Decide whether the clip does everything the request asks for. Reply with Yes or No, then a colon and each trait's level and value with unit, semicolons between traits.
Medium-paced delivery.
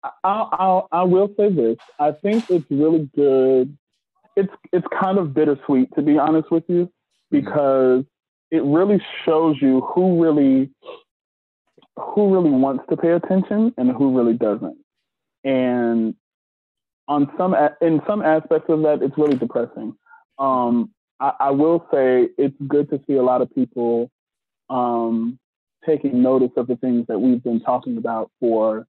Yes: average, 150 wpm